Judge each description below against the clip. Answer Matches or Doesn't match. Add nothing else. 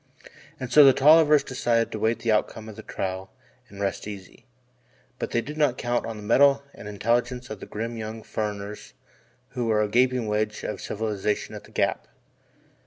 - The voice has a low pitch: Matches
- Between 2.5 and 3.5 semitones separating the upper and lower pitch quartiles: Matches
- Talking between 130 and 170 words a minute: Doesn't match